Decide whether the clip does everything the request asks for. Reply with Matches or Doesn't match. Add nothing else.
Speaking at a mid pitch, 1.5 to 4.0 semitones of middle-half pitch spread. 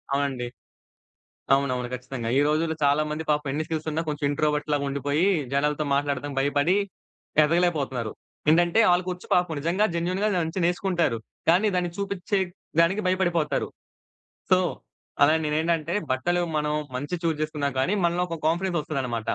Matches